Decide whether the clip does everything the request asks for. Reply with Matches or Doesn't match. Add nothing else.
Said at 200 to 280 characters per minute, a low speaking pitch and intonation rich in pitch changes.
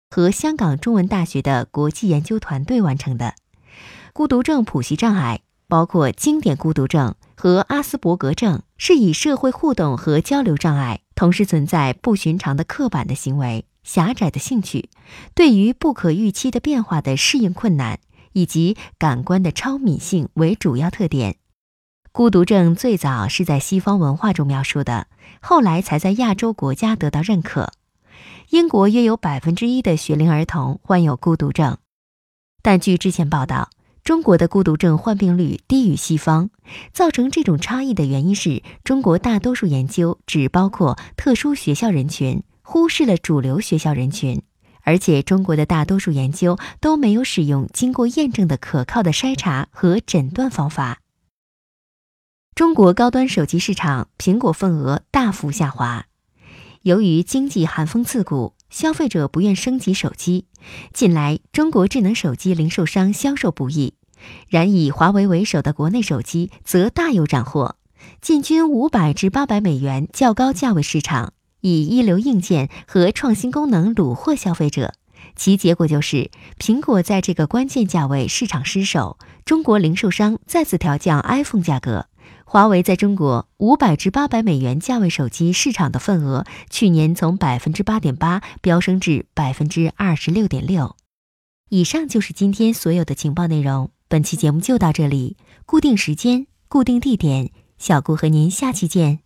Doesn't match